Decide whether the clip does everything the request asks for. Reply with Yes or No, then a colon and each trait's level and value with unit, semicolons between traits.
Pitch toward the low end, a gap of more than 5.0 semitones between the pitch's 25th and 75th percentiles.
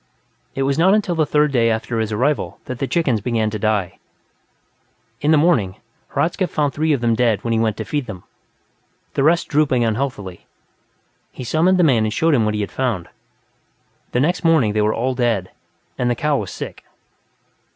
Yes: low, 125 Hz; wide, 5.5 semitones